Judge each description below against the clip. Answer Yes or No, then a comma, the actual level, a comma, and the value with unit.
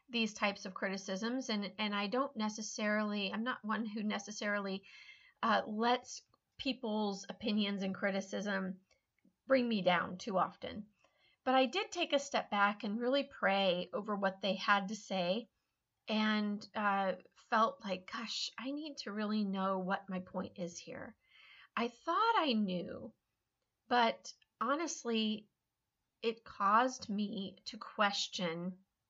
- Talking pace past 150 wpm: No, average, 140 wpm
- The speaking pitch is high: Yes, high, 210 Hz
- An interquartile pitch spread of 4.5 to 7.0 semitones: No, average, 3.4 semitones